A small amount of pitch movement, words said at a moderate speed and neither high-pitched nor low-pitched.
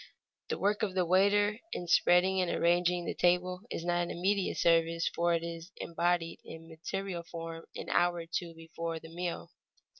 Yes: narrow, 1.5 semitones; average, 180 wpm; medium, 175 Hz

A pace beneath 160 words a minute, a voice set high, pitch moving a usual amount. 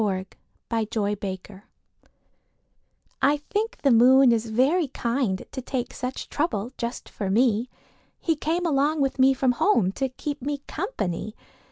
Yes: average, 150 wpm; very high, 255 Hz; average, 4.5 semitones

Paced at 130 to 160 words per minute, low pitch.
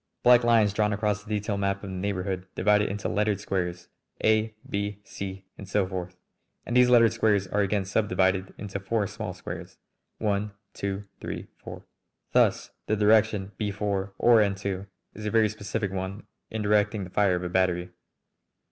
No: average, 180 wpm; low, 100 Hz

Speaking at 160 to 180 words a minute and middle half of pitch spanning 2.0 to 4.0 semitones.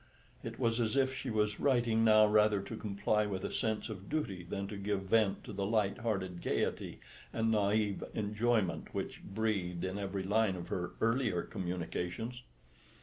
Yes: average, 170 wpm; narrow, 2.6 semitones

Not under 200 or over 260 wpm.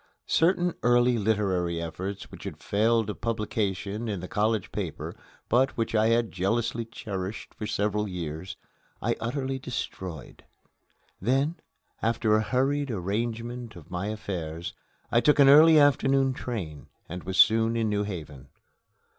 No: average, 140 wpm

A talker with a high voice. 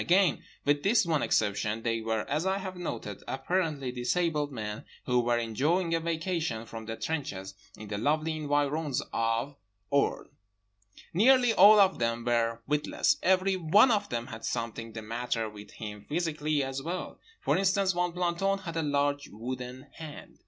No: medium, 145 Hz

